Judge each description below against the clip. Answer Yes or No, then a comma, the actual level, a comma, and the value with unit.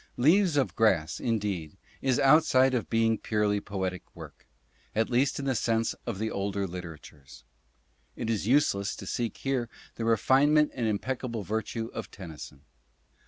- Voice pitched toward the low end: Yes, low, 115 Hz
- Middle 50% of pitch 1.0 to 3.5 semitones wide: No, average, 4.6 semitones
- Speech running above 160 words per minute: No, average, 155 wpm